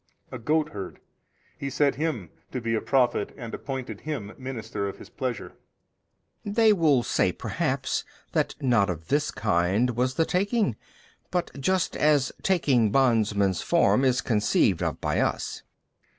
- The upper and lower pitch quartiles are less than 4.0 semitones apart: No, wide, 5.6 semitones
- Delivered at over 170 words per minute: No, average, 150 wpm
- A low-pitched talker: Yes, low, 130 Hz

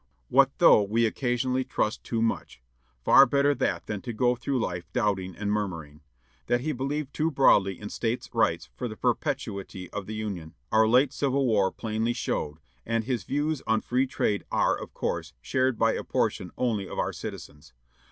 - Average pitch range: Yes, average, 4.6 semitones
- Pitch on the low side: Yes, low, 115 Hz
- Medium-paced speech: Yes, average, 180 wpm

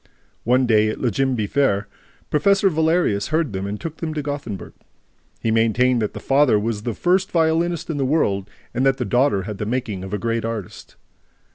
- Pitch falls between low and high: No, low, 125 Hz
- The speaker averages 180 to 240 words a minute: Yes, average, 190 wpm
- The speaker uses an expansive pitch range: Yes, wide, 6.1 semitones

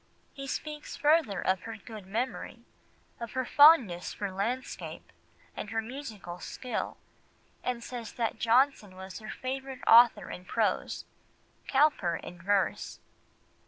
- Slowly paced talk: Yes, slow, 125 wpm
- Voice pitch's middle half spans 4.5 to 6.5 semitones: Yes, average, 5.0 semitones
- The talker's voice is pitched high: Yes, high, 230 Hz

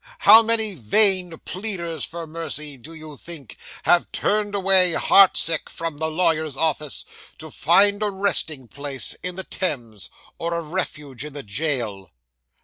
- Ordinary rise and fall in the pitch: Yes, average, 4.5 semitones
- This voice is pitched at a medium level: Yes, medium, 165 Hz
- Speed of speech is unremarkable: Yes, average, 150 wpm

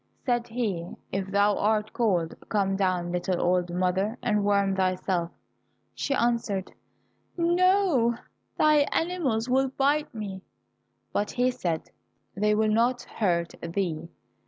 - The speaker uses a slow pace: Yes, slow, 125 wpm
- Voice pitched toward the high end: Yes, high, 210 Hz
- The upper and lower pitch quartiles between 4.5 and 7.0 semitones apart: Yes, average, 4.8 semitones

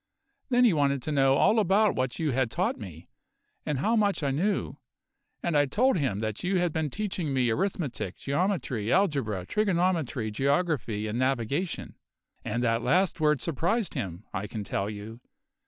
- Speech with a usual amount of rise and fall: No, wide, 7.9 semitones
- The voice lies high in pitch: No, medium, 140 Hz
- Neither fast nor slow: Yes, average, 170 wpm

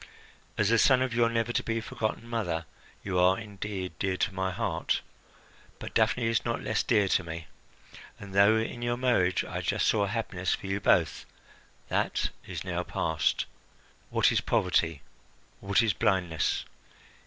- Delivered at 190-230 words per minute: No, average, 165 wpm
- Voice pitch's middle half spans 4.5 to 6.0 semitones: No, average, 3.8 semitones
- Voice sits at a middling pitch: No, low, 100 Hz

